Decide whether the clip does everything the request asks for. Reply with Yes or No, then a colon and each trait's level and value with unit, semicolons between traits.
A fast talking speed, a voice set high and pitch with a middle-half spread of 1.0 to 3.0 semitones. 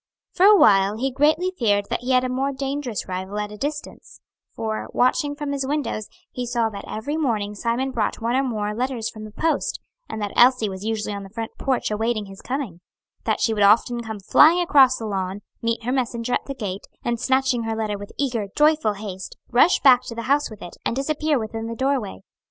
No: fast, 220 wpm; high, 235 Hz; average, 4.2 semitones